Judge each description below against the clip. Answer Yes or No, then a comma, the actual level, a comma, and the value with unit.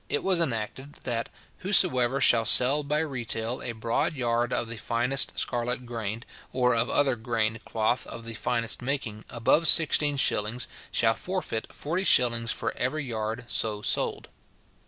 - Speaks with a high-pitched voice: No, low, 120 Hz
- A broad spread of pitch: No, average, 3.4 semitones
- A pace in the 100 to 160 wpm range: Yes, average, 155 wpm